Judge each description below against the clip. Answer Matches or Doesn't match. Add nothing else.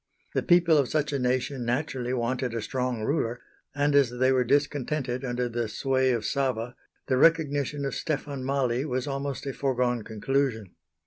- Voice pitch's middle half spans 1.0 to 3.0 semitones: Matches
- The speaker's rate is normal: Matches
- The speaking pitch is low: Matches